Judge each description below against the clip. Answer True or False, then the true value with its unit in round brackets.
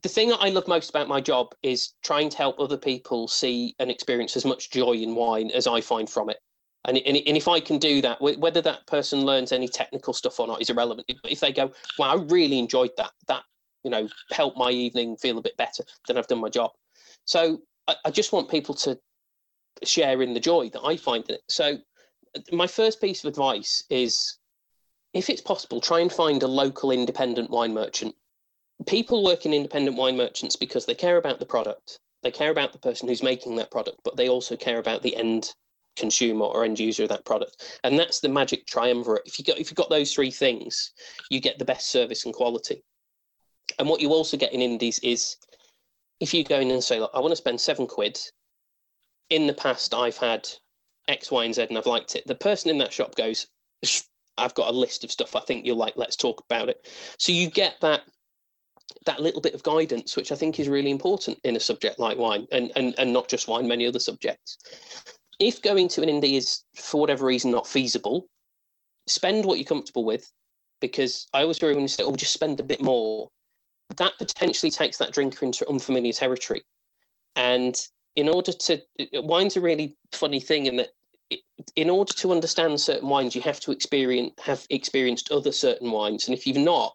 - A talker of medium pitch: True (145 Hz)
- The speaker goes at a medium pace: False (215 wpm)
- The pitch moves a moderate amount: False (7.7 semitones)